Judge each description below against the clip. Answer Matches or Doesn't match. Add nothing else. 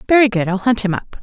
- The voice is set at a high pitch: Matches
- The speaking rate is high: Matches